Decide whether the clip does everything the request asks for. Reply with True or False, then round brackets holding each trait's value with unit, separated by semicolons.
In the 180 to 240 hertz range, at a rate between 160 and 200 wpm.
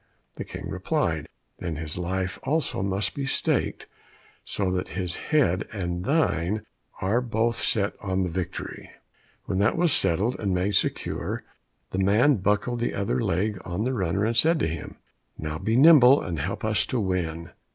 False (100 Hz; 170 wpm)